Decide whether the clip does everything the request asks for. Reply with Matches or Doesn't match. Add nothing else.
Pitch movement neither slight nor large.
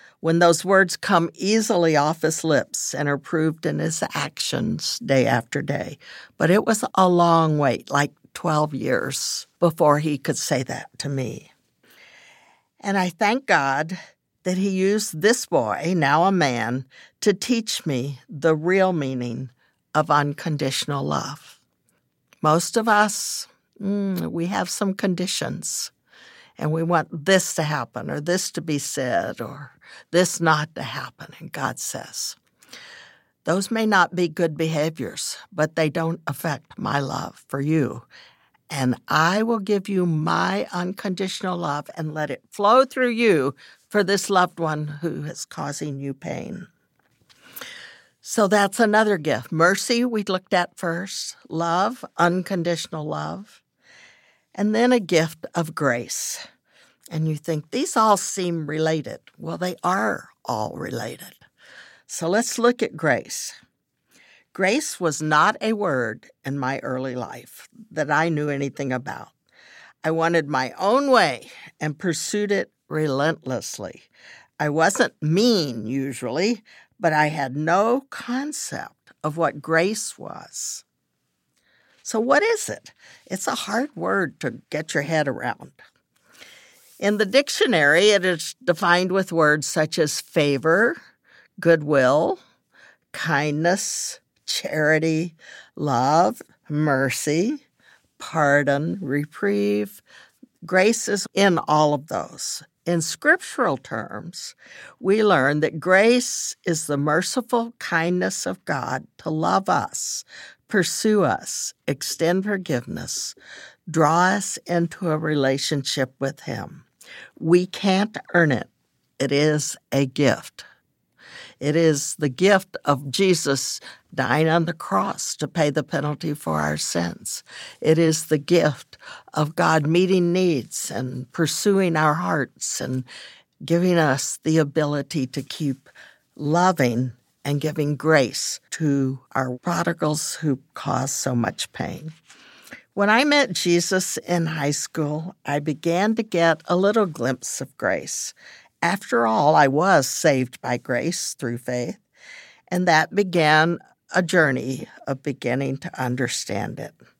Matches